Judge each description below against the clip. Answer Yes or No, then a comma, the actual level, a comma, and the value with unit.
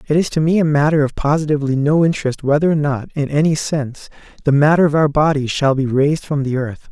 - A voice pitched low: No, medium, 145 Hz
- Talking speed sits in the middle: No, fast, 235 wpm